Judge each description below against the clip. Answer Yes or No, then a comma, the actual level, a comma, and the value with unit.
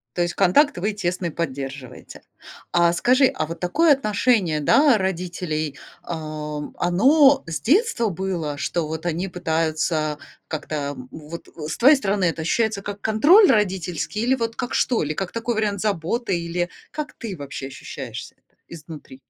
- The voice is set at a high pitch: No, medium, 175 Hz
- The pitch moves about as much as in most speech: No, wide, 5.7 semitones